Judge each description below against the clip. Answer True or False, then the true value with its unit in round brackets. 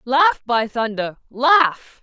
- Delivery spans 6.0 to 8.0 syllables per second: False (2.9 syllables/s)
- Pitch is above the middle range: True (250 Hz)